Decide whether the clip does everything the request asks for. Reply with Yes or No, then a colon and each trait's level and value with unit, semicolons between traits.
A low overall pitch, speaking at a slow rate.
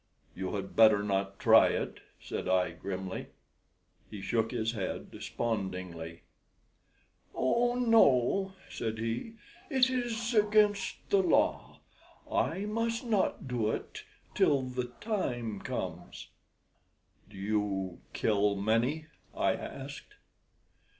Yes: low, 115 Hz; slow, 110 wpm